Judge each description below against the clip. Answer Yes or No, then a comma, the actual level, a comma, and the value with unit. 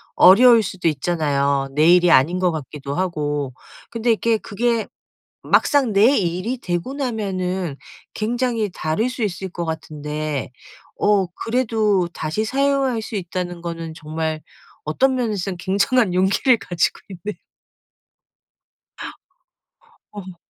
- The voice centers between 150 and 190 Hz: Yes, medium, 185 Hz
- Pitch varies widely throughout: Yes, wide, 5.7 semitones